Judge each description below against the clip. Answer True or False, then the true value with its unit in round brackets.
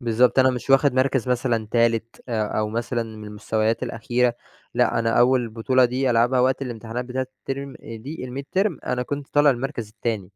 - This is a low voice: True (120 Hz)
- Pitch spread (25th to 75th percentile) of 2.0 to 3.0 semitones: True (2.4 semitones)